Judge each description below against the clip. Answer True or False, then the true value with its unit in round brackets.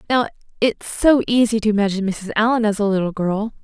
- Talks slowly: False (200 wpm)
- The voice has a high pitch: True (215 Hz)